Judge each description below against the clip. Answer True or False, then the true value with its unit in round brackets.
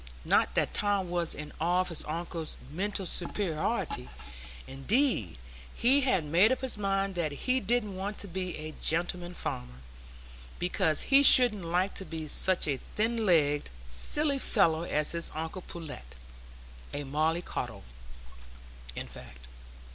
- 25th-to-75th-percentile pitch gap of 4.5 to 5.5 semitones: True (5.0 semitones)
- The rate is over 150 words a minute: False (140 wpm)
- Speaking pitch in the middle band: True (175 Hz)